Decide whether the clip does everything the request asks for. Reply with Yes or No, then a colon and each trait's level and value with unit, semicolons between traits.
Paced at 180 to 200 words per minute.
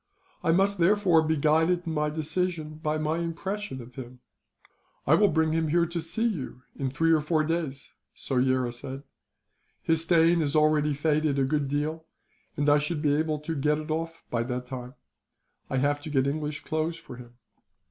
Yes: average, 185 wpm